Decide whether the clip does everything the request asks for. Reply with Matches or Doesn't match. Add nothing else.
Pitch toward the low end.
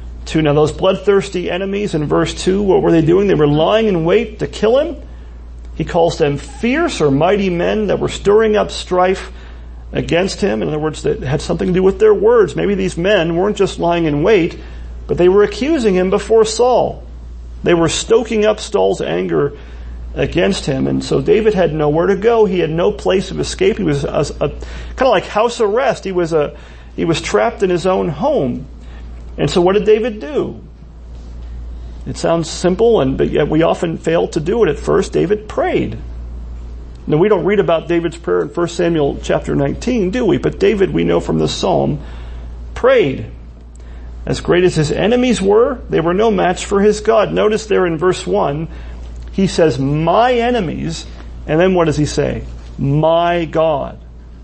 Doesn't match